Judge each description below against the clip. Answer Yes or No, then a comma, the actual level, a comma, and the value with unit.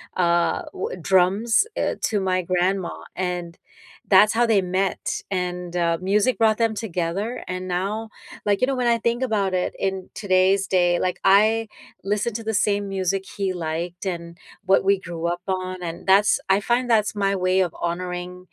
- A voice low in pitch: No, high, 190 Hz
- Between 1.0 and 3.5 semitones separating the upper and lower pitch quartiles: Yes, narrow, 2.6 semitones